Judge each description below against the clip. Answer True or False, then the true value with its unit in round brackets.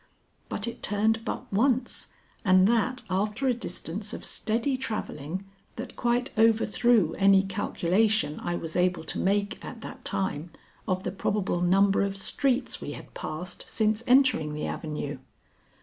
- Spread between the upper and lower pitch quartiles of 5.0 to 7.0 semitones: False (4.1 semitones)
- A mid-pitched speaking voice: False (205 Hz)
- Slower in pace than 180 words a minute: True (150 wpm)